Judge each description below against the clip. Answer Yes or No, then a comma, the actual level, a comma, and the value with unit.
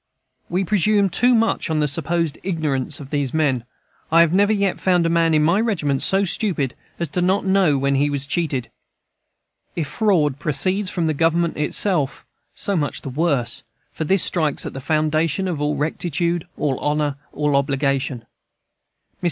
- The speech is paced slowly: No, average, 170 wpm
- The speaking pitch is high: No, medium, 160 Hz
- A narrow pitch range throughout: No, average, 4.1 semitones